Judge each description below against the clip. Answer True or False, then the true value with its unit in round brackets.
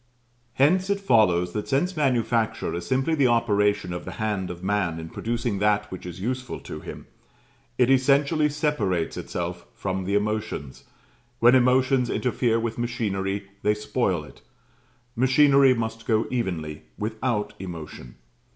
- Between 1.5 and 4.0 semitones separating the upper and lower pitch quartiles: False (5.2 semitones)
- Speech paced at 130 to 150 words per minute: True (140 wpm)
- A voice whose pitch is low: True (110 Hz)